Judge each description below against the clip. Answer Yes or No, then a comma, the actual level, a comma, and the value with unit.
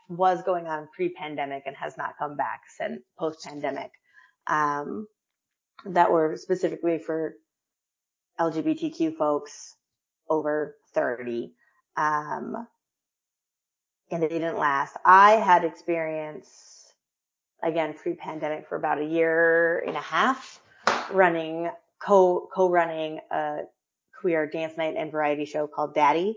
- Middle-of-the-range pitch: Yes, medium, 165 Hz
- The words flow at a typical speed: No, slow, 110 wpm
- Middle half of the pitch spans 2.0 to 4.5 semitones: Yes, average, 2.9 semitones